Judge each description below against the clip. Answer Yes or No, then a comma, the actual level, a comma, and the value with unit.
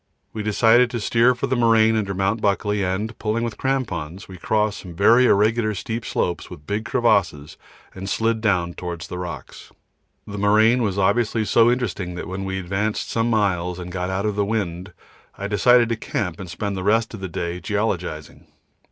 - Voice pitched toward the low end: Yes, low, 105 Hz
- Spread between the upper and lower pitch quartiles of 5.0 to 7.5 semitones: No, average, 3.4 semitones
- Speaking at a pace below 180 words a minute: No, average, 195 wpm